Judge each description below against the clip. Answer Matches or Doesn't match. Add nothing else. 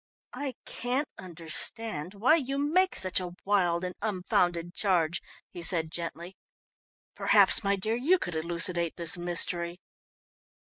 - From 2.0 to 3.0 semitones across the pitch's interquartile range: Doesn't match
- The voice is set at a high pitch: Doesn't match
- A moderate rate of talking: Doesn't match